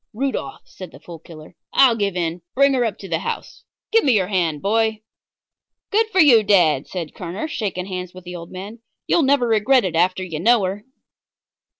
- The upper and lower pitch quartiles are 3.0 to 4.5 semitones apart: No, average, 5.2 semitones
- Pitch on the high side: Yes, high, 195 Hz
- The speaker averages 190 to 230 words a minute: Yes, average, 200 wpm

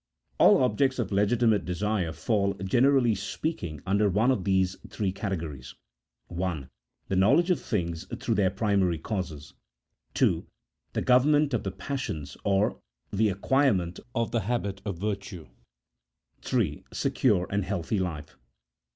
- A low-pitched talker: Yes, low, 100 Hz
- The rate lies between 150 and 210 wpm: No, slow, 135 wpm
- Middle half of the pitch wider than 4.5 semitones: No, average, 4.2 semitones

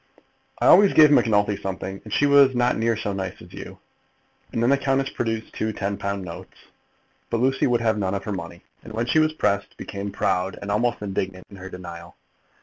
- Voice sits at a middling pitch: No, low, 105 Hz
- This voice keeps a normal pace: No, fast, 210 wpm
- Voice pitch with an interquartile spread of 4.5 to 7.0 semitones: No, average, 3.9 semitones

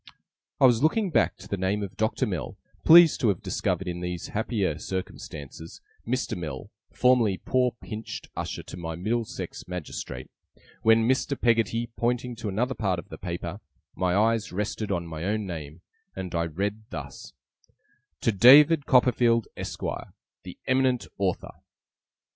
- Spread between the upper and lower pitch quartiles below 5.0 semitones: No, average, 5.3 semitones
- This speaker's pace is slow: No, average, 150 wpm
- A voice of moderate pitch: No, low, 105 Hz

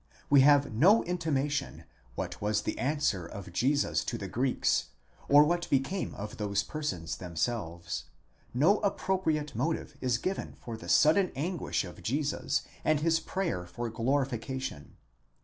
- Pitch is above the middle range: No, low, 135 Hz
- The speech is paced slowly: No, average, 145 wpm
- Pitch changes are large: Yes, wide, 6.4 semitones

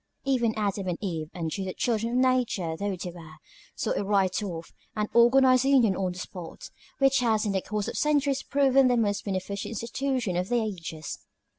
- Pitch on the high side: Yes, high, 210 Hz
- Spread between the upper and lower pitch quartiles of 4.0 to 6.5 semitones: Yes, average, 5.3 semitones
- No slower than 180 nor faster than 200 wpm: Yes, average, 190 wpm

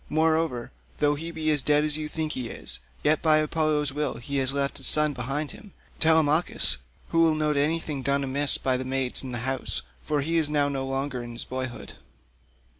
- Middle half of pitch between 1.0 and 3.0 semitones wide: Yes, narrow, 2.6 semitones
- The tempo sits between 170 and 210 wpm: Yes, average, 200 wpm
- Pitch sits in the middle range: Yes, medium, 145 Hz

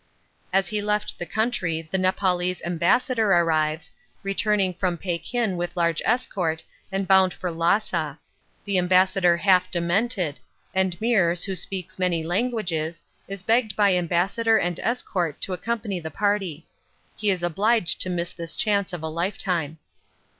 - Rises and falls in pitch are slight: No, average, 3.0 semitones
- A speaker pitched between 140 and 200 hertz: Yes, medium, 185 Hz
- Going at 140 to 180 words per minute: Yes, average, 145 wpm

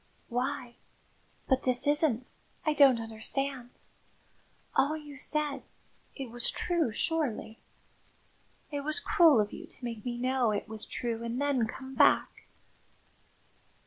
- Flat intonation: No, average, 3.6 semitones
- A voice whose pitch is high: Yes, very high, 260 Hz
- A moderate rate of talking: No, slow, 130 wpm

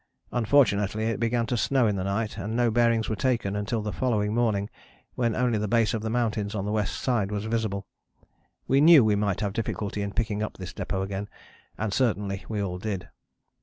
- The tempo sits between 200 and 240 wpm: Yes, fast, 205 wpm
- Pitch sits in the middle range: No, low, 110 Hz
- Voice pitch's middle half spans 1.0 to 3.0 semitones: Yes, narrow, 2.5 semitones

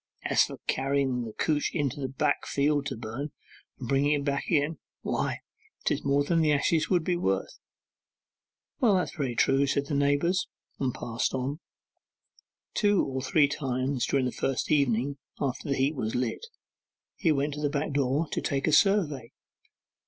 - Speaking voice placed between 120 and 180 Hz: Yes, medium, 140 Hz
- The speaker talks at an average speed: Yes, average, 175 wpm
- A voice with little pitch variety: Yes, narrow, 2.3 semitones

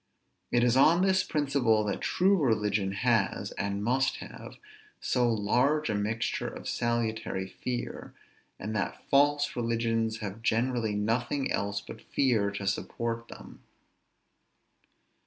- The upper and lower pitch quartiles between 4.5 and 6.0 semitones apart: No, average, 3.6 semitones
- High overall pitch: No, low, 115 Hz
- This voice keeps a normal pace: No, slow, 125 wpm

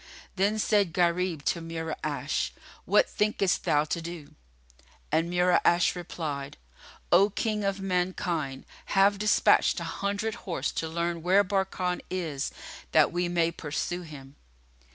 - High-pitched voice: No, medium, 175 Hz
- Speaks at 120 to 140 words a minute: Yes, slow, 135 wpm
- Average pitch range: Yes, average, 3.0 semitones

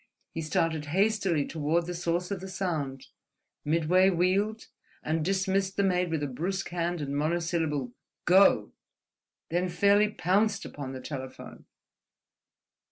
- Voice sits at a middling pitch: Yes, medium, 175 Hz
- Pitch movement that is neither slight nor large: Yes, average, 3.7 semitones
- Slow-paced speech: Yes, slow, 120 wpm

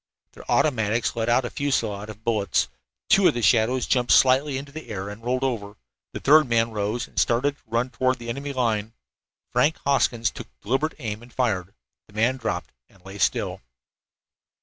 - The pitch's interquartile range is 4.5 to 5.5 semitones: No, average, 3.3 semitones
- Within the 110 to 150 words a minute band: No, average, 190 wpm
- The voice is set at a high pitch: No, low, 120 Hz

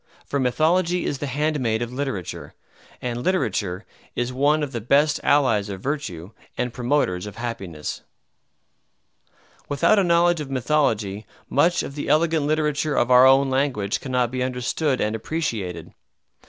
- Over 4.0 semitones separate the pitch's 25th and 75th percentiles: Yes, average, 4.8 semitones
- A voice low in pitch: Yes, low, 130 Hz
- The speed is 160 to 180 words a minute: No, average, 145 wpm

